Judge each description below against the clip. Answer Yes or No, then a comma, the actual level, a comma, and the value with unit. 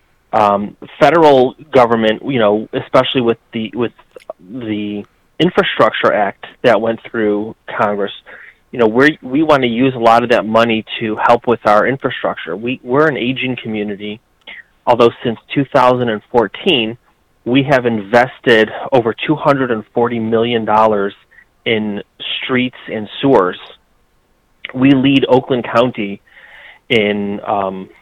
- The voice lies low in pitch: Yes, low, 115 Hz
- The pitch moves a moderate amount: Yes, average, 3.3 semitones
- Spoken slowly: Yes, slow, 120 wpm